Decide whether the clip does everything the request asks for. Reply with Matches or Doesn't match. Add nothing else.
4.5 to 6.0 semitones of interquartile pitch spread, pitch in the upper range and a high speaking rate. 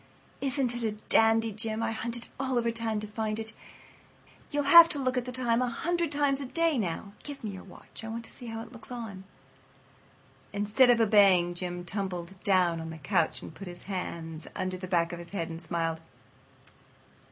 Matches